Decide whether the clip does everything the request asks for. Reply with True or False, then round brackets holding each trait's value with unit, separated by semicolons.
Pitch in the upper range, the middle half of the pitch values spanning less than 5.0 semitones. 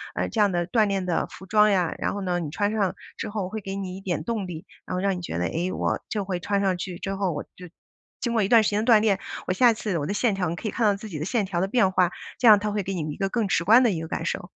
True (195 Hz; 2.7 semitones)